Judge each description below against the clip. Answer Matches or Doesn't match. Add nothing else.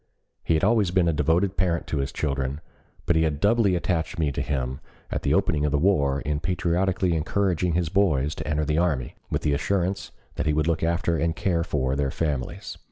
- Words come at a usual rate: Doesn't match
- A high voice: Doesn't match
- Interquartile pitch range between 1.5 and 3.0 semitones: Doesn't match